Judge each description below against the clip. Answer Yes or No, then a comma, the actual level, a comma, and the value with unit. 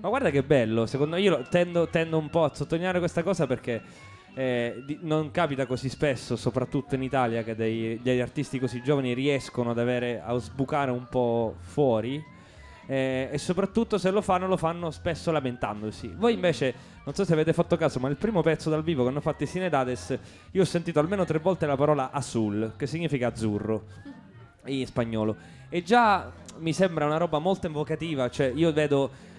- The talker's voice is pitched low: No, medium, 145 Hz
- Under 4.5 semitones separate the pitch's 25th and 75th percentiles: No, average, 5.1 semitones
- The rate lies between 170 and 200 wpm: Yes, average, 190 wpm